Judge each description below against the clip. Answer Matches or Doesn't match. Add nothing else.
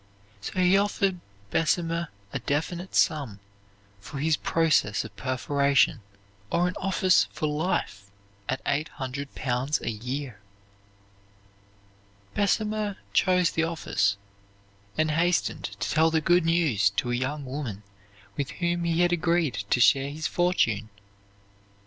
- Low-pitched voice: Doesn't match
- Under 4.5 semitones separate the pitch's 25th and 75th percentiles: Doesn't match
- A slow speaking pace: Matches